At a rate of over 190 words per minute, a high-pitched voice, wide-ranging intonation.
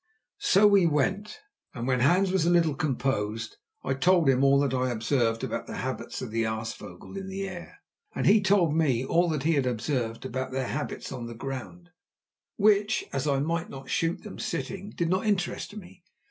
No: average, 200 wpm; medium, 150 Hz; wide, 6.4 semitones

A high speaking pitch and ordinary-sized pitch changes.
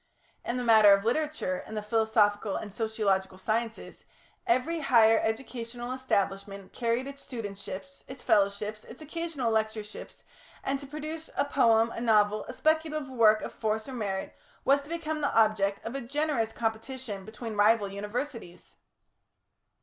Yes: high, 225 Hz; average, 4.2 semitones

